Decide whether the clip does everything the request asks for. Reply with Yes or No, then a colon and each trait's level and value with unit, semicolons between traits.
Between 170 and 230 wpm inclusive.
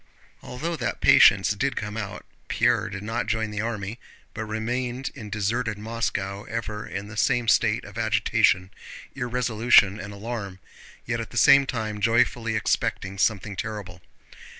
No: average, 150 wpm